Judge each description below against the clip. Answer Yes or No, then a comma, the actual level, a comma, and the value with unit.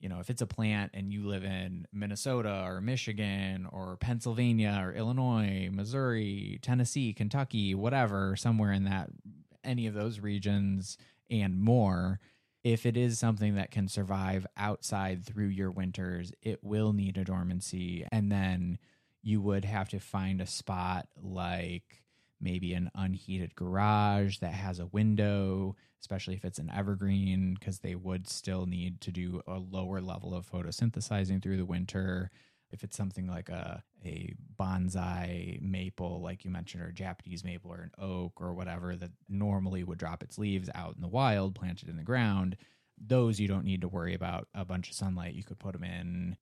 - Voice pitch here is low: Yes, very low, 95 Hz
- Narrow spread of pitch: Yes, narrow, 2.3 semitones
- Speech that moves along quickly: No, average, 170 wpm